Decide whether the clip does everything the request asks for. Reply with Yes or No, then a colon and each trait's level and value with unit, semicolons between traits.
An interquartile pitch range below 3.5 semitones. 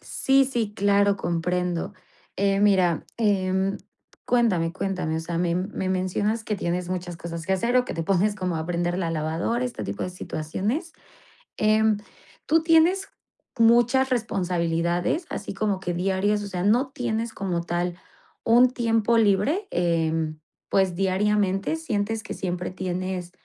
No: average, 4.2 semitones